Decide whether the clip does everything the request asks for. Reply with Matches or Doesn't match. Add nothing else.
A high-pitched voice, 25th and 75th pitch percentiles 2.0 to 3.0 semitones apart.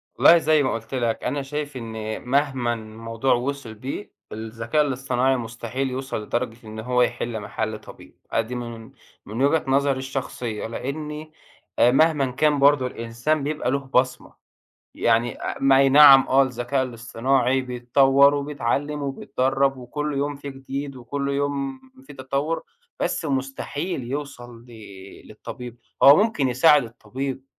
Doesn't match